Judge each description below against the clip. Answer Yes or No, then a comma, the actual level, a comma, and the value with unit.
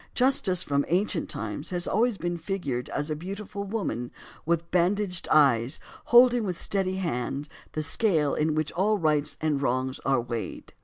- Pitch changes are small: No, wide, 5.5 semitones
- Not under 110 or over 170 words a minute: Yes, average, 160 wpm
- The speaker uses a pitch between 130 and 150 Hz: No, medium, 170 Hz